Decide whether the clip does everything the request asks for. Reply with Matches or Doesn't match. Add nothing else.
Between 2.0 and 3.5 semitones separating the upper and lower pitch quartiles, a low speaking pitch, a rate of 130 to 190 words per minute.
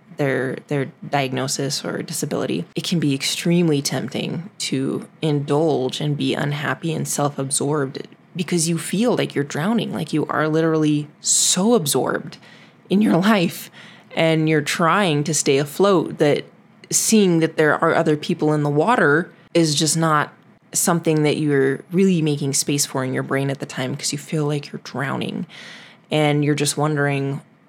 Doesn't match